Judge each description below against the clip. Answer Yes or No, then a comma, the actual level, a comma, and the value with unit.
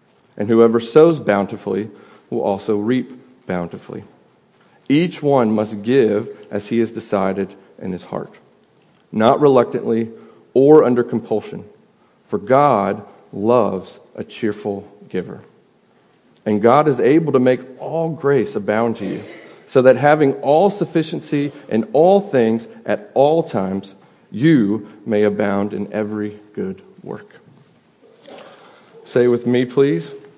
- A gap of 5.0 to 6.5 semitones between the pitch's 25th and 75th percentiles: Yes, average, 5.3 semitones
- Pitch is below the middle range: Yes, low, 115 Hz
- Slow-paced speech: Yes, slow, 125 wpm